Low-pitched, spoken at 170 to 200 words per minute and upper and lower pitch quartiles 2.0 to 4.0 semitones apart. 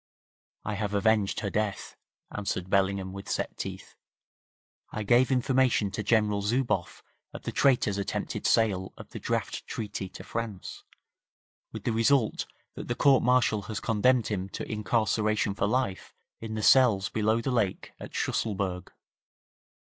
No: low, 110 Hz; average, 150 wpm; average, 2.8 semitones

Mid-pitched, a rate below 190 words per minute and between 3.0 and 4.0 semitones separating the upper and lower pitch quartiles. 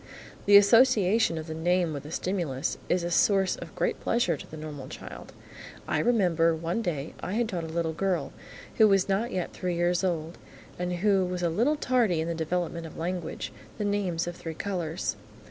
No: medium, 175 Hz; average, 195 wpm; average, 3.5 semitones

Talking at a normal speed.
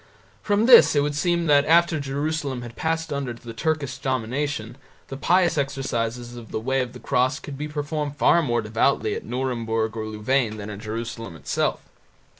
Yes: average, 180 wpm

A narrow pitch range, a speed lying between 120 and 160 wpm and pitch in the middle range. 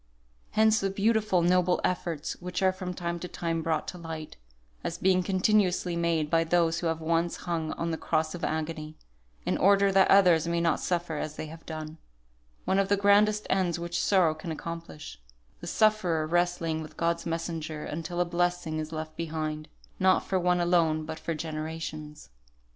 No: narrow, 2.3 semitones; average, 180 wpm; medium, 170 Hz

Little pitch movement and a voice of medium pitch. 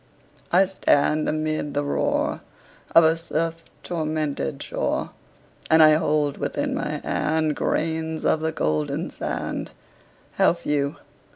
Yes: narrow, 1.4 semitones; medium, 155 Hz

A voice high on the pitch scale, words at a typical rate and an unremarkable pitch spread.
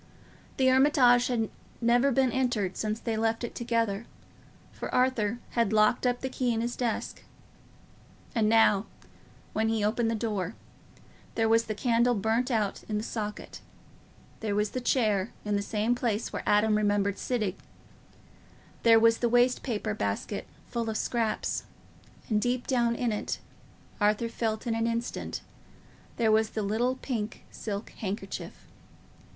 No: high, 225 Hz; average, 155 wpm; narrow, 2.3 semitones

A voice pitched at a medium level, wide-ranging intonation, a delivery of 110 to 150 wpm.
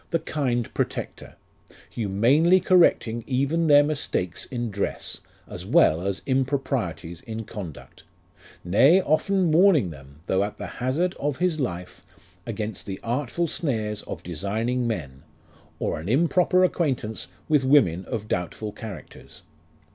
No: low, 120 Hz; wide, 7.5 semitones; slow, 135 wpm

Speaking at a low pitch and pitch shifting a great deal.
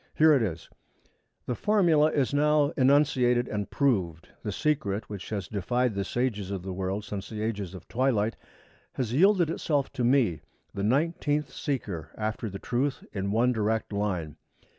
Yes: low, 115 Hz; wide, 5.9 semitones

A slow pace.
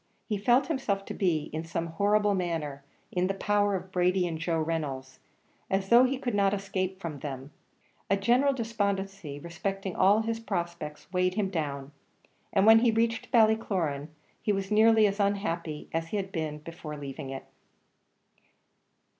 No: average, 165 wpm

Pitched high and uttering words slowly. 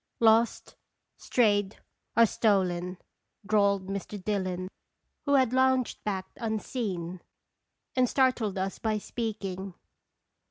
Yes: high, 205 Hz; slow, 95 wpm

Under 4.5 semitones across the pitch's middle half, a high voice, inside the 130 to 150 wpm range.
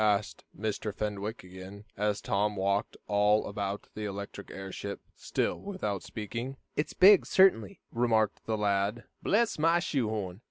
No: average, 2.7 semitones; low, 105 Hz; average, 145 wpm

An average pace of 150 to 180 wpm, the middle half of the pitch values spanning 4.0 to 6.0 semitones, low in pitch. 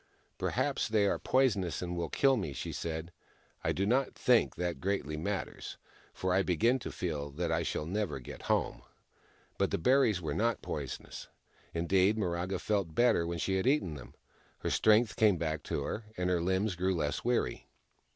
No: average, 190 wpm; average, 4.5 semitones; very low, 90 Hz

